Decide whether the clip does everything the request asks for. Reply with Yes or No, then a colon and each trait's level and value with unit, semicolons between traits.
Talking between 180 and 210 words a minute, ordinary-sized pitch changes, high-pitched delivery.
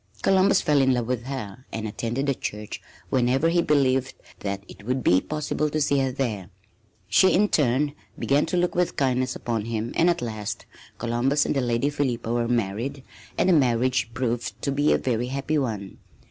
No: average, 190 wpm; average, 3.7 semitones; low, 130 Hz